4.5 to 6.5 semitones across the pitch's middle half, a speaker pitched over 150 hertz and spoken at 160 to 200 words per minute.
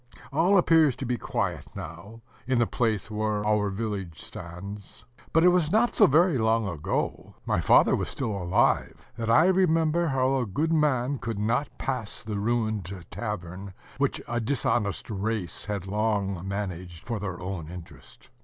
No: average, 5.3 semitones; low, 110 Hz; average, 165 wpm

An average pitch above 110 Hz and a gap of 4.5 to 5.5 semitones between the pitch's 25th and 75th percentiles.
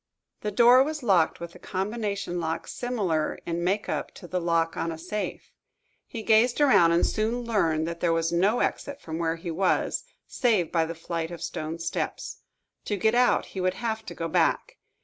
Yes: medium, 185 Hz; average, 4.9 semitones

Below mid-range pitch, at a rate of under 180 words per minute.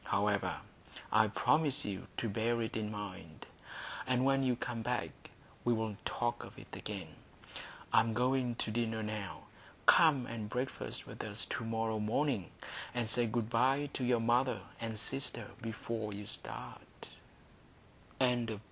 Yes: low, 115 Hz; average, 150 wpm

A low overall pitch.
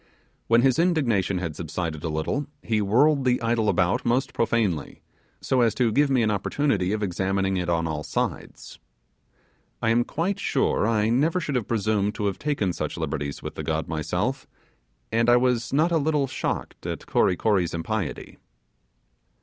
Yes: low, 110 Hz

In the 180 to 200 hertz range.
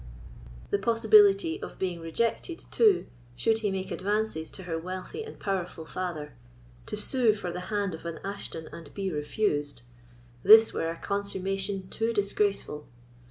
Yes: high, 190 Hz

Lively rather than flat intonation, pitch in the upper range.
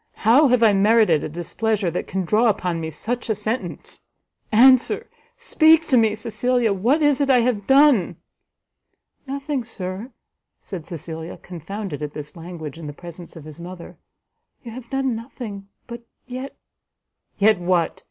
Yes: wide, 6.3 semitones; high, 215 Hz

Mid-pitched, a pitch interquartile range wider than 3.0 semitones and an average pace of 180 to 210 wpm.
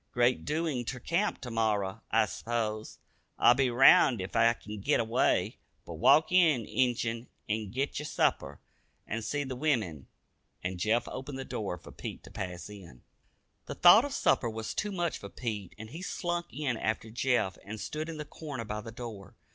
No: low, 120 Hz; average, 5.0 semitones; average, 185 wpm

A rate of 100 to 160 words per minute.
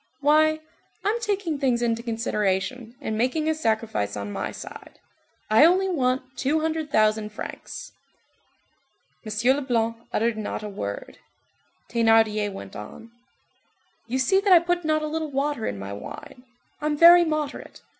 Yes: average, 145 wpm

